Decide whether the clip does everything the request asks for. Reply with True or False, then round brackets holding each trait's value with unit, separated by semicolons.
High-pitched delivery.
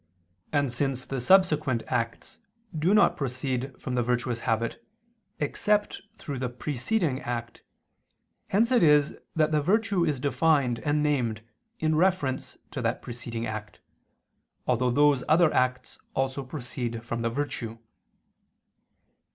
False (135 Hz)